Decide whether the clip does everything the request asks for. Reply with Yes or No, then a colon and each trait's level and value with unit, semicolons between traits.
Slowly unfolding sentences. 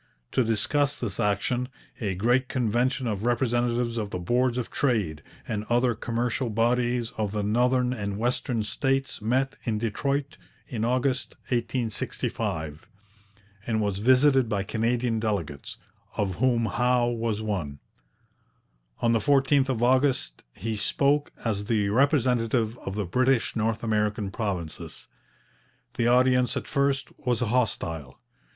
Yes: slow, 130 wpm